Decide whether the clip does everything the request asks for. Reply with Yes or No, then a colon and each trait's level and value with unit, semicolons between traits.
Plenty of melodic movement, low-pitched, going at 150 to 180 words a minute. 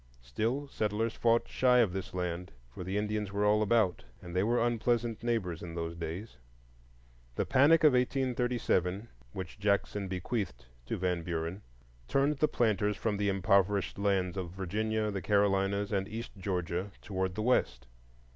No: average, 3.8 semitones; low, 100 Hz; average, 155 wpm